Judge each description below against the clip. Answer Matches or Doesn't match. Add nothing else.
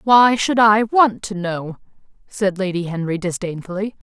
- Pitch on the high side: Matches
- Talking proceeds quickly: Doesn't match